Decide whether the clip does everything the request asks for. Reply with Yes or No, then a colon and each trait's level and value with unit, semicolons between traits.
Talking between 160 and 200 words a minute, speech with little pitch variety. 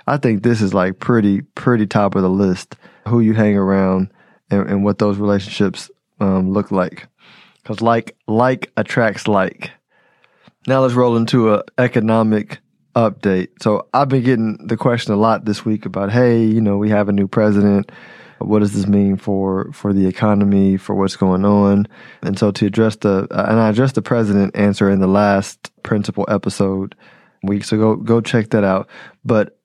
Yes: average, 185 wpm; narrow, 2.3 semitones